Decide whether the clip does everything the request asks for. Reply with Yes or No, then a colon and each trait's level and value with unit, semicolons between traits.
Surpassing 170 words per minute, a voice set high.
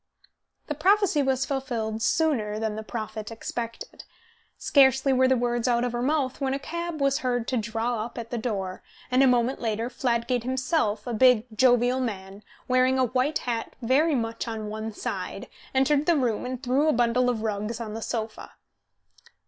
Yes: average, 180 wpm; high, 245 Hz